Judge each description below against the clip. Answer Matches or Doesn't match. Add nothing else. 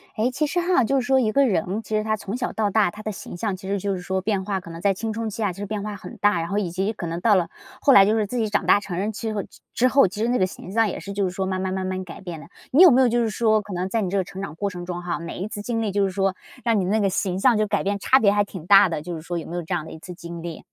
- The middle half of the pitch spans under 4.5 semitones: Matches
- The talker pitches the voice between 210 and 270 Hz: Doesn't match